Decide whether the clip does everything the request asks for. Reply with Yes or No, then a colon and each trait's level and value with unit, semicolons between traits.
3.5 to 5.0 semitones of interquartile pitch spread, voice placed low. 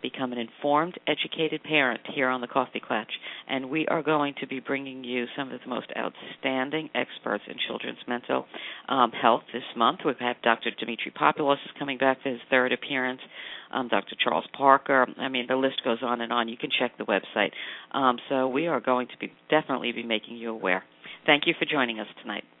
No: average, 2.7 semitones; low, 130 Hz